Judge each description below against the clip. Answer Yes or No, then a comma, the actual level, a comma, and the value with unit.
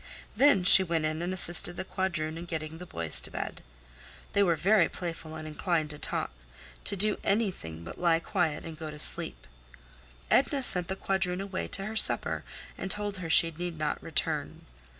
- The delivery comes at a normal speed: Yes, average, 185 wpm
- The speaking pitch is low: No, medium, 175 Hz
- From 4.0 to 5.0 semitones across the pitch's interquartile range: No, average, 3.5 semitones